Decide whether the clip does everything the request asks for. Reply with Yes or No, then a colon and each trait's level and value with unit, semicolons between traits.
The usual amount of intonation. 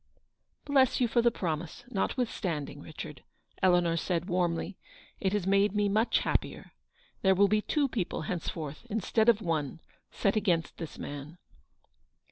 Yes: average, 4.5 semitones